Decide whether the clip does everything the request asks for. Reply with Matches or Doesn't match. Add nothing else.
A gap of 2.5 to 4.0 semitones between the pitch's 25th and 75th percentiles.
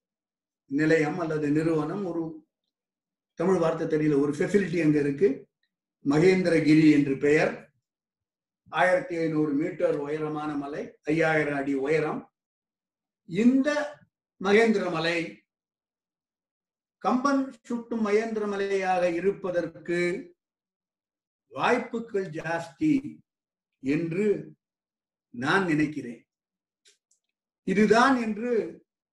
Doesn't match